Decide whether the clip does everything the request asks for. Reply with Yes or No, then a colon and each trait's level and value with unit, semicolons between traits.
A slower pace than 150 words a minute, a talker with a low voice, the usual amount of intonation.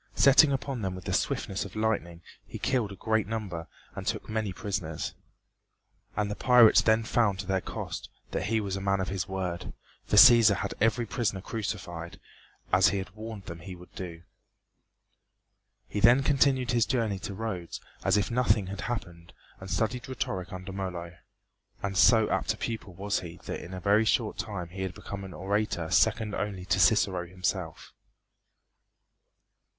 No: average, 175 wpm; low, 100 Hz; average, 3.3 semitones